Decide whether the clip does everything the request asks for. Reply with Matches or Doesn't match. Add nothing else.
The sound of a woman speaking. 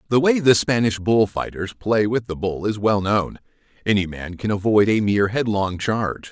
Doesn't match